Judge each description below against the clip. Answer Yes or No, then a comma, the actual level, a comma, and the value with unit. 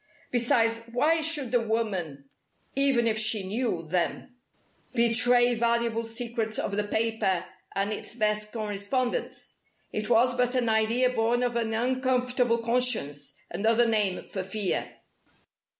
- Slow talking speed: Yes, slow, 130 wpm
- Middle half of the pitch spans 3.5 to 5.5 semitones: No, narrow, 2.5 semitones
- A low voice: No, high, 230 Hz